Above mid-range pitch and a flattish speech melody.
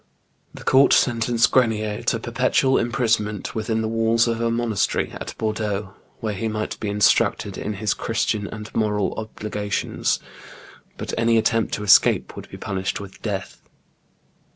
No: low, 110 Hz; narrow, 1.7 semitones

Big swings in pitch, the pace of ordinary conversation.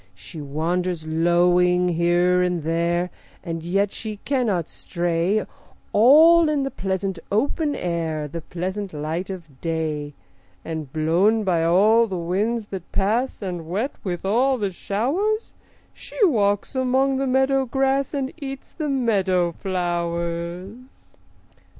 No: wide, 6.0 semitones; slow, 130 wpm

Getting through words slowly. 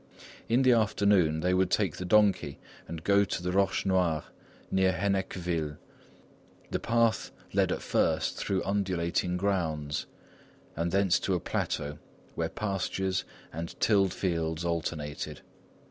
Yes: slow, 130 wpm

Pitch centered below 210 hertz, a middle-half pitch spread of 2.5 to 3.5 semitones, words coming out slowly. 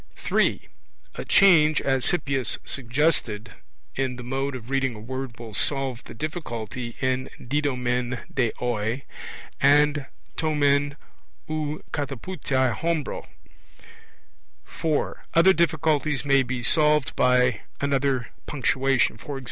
Yes: low, 135 Hz; average, 3.0 semitones; slow, 115 wpm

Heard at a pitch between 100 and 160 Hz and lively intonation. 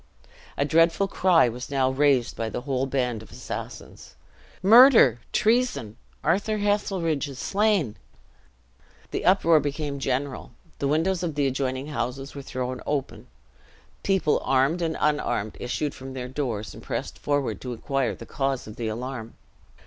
No: medium, 140 Hz; average, 4.5 semitones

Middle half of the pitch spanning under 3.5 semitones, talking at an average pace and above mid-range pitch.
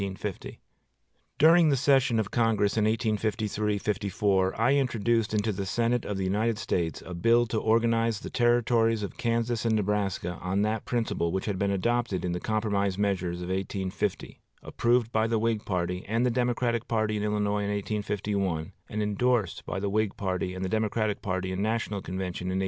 No: average, 3.0 semitones; average, 180 wpm; low, 105 Hz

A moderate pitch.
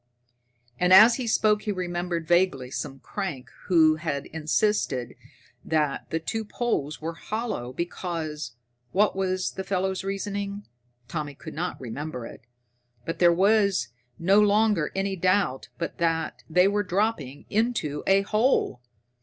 Yes: medium, 180 Hz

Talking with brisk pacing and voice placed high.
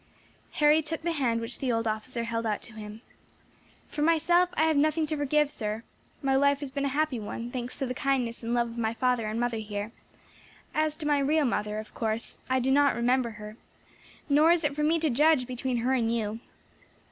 Yes: fast, 215 wpm; very high, 255 Hz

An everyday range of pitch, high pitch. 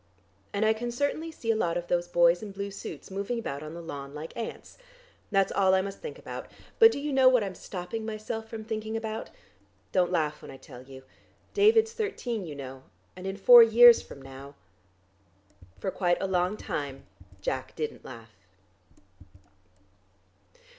No: wide, 7.1 semitones; high, 195 Hz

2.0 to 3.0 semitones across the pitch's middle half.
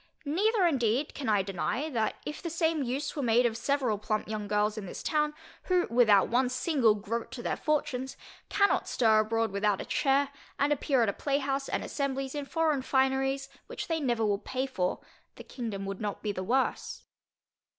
No: average, 4.7 semitones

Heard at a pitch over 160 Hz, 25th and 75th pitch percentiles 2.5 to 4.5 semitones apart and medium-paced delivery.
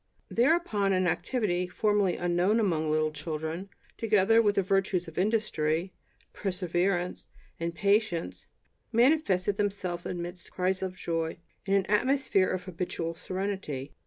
No: medium, 185 Hz; average, 3.0 semitones; slow, 125 wpm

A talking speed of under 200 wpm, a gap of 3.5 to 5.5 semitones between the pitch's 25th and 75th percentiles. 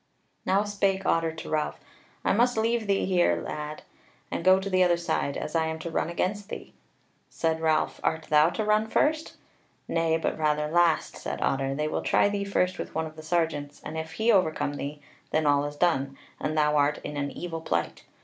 No: fast, 205 wpm; average, 4.0 semitones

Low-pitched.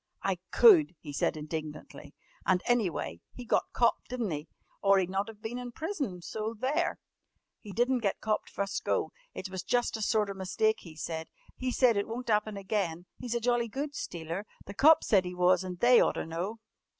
No: high, 210 Hz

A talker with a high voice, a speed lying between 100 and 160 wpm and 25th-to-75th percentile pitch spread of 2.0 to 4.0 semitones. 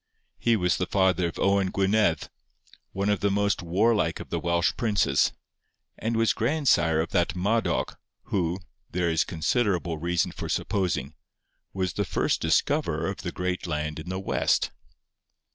No: very low, 95 Hz; average, 155 wpm; average, 3.1 semitones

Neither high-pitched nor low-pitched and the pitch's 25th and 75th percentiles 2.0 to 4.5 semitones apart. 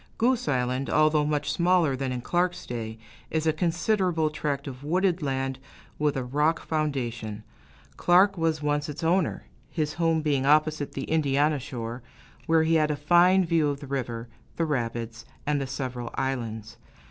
Yes: medium, 150 Hz; average, 3.6 semitones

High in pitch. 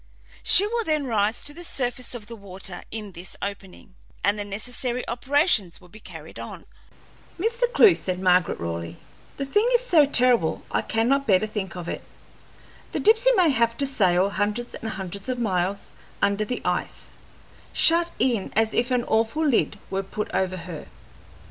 Yes: high, 225 Hz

